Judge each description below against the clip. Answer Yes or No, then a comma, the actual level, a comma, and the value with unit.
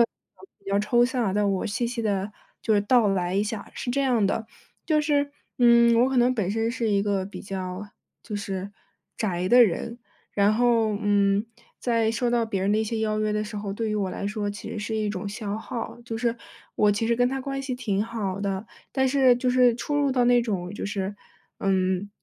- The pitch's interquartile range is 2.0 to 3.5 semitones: Yes, average, 3.2 semitones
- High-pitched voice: Yes, high, 215 Hz